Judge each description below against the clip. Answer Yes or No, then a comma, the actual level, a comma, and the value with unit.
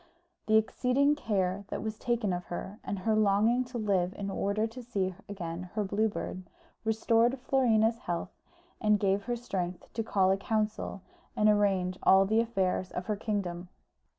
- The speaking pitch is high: Yes, high, 205 Hz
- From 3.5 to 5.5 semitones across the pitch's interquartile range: No, average, 2.9 semitones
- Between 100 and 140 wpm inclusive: No, average, 170 wpm